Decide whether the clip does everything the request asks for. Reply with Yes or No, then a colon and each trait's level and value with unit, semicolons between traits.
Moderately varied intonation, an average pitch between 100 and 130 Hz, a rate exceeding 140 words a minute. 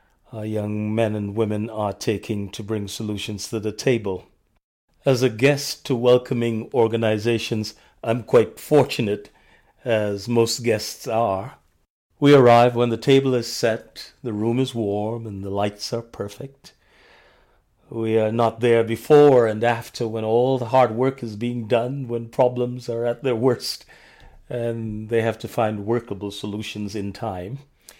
No: narrow, 2.3 semitones; low, 115 Hz; average, 155 wpm